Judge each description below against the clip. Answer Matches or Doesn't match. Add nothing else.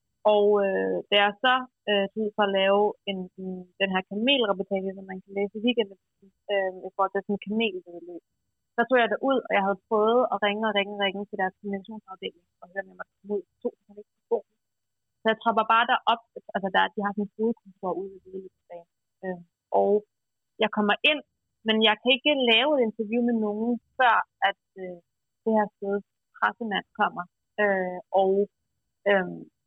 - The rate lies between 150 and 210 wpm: Matches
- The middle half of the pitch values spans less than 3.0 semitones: Matches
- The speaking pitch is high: Matches